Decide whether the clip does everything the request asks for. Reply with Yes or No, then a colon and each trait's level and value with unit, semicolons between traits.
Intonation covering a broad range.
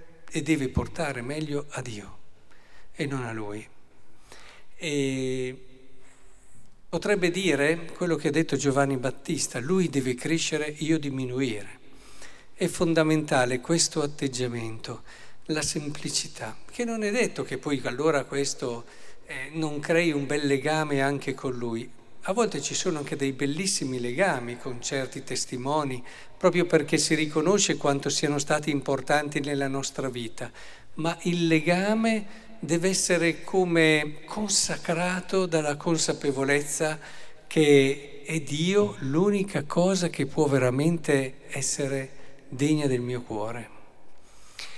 No: average, 3.6 semitones